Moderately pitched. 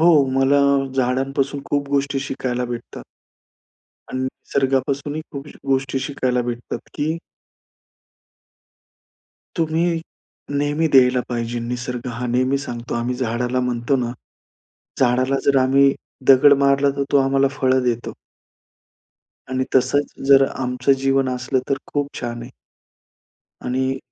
No: low, 130 Hz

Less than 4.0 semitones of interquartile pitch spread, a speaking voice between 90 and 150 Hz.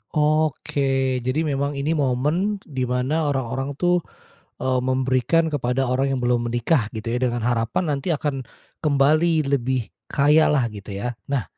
Yes: average, 3.5 semitones; low, 135 Hz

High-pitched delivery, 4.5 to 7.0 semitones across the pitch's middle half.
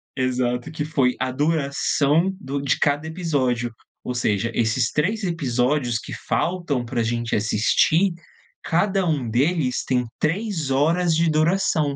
No: medium, 145 Hz; average, 5.1 semitones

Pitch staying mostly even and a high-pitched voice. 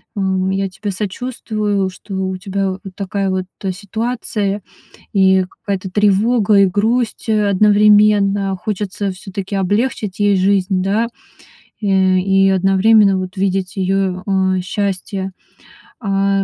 Yes: narrow, 1.6 semitones; high, 195 Hz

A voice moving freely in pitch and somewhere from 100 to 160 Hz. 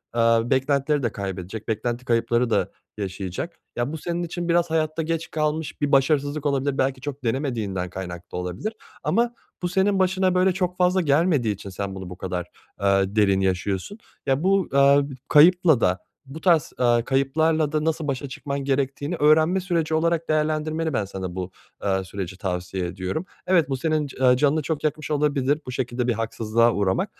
Yes: wide, 7.1 semitones; medium, 140 Hz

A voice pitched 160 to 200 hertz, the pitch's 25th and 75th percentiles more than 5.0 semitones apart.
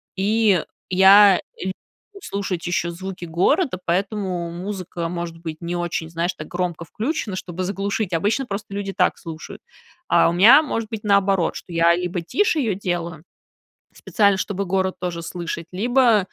No: medium, 185 Hz; average, 3.0 semitones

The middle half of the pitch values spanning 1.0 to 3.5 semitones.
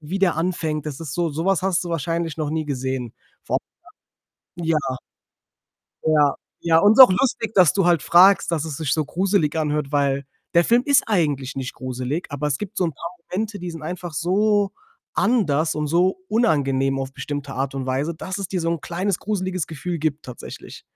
No: average, 4.3 semitones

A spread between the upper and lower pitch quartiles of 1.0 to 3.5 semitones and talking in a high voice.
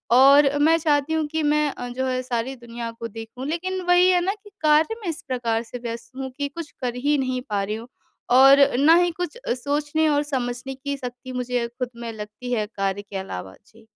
No: average, 4.2 semitones; very high, 260 Hz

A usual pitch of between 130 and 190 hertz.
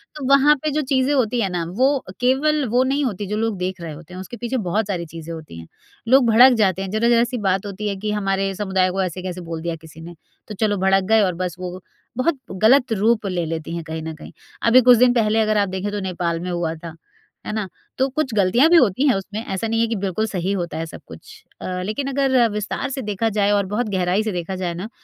No: high, 205 Hz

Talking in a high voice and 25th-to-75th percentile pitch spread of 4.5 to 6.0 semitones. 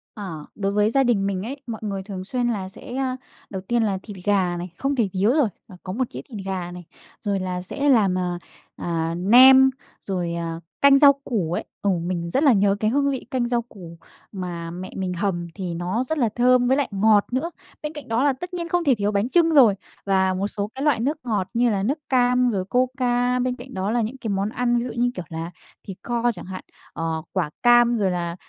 Yes: high, 210 Hz; average, 5.1 semitones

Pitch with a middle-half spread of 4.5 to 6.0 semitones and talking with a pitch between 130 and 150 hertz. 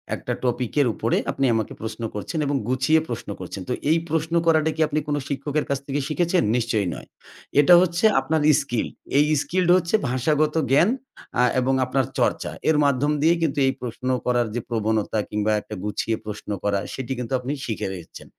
Yes: average, 5.1 semitones; low, 135 Hz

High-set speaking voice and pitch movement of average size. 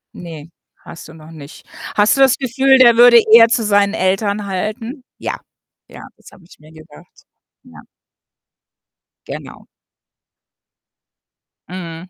No: high, 200 Hz; wide, 6.0 semitones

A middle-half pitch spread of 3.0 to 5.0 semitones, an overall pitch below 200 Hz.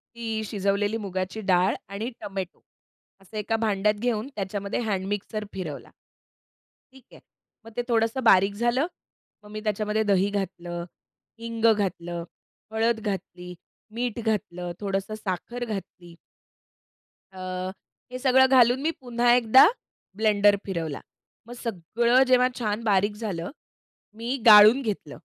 No: average, 3.3 semitones; high, 210 Hz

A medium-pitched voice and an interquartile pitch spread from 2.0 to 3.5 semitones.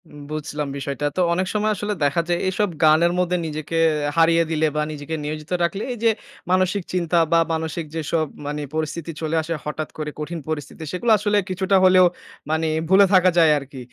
Yes: medium, 165 Hz; average, 3.2 semitones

